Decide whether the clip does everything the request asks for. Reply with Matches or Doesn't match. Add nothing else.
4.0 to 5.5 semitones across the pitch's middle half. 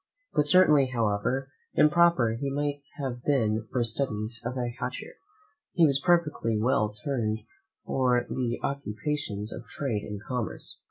Matches